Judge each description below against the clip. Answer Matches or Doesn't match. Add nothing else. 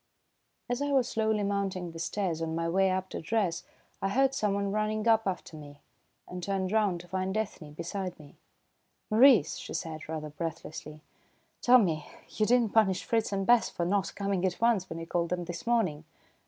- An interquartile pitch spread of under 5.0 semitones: Matches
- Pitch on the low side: Doesn't match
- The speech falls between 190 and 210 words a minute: Matches